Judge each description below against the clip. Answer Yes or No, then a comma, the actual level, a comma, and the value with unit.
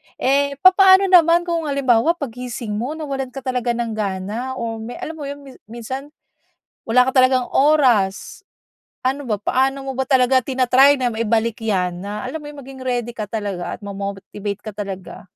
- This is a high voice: Yes, very high, 250 Hz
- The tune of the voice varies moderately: Yes, average, 4.2 semitones